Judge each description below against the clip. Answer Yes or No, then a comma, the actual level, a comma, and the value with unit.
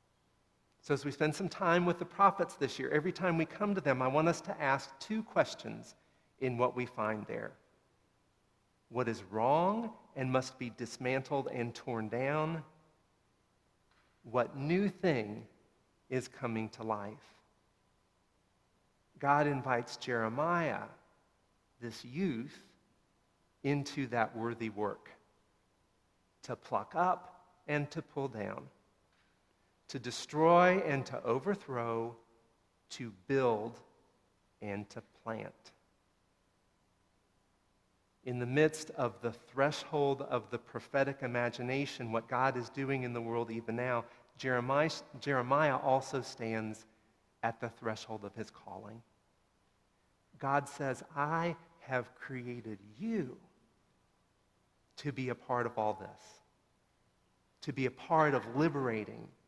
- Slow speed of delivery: Yes, slow, 120 wpm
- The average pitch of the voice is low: Yes, low, 125 Hz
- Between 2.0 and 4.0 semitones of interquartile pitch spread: No, average, 4.5 semitones